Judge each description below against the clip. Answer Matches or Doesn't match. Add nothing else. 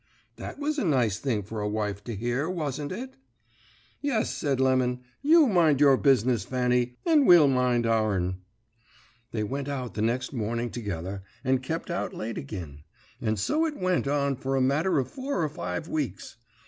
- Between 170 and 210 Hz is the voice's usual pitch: Doesn't match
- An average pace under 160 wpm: Doesn't match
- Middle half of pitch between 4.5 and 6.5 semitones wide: Matches